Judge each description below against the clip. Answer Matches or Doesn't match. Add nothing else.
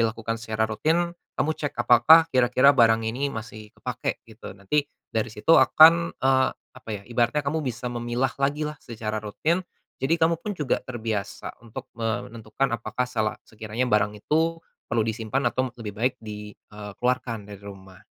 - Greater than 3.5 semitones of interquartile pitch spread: Matches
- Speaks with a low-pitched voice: Matches